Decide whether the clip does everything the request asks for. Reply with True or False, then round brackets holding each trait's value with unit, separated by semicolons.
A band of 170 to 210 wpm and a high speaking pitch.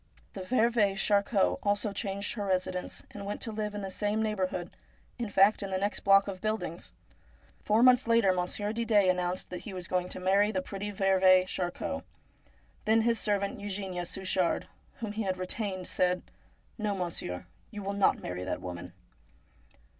True (175 wpm; 195 Hz)